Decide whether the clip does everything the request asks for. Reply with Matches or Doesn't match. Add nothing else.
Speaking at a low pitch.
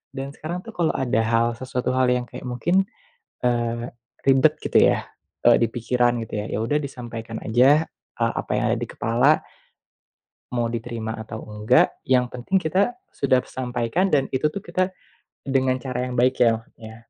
Matches